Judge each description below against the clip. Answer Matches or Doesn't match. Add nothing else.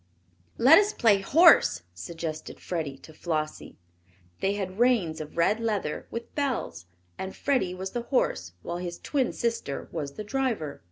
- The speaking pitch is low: Doesn't match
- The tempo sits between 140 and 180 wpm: Matches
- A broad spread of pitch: Matches